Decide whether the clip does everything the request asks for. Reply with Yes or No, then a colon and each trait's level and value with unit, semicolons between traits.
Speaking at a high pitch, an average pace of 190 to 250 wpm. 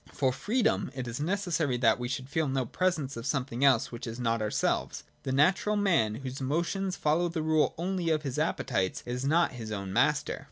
No: low, 135 Hz; average, 200 wpm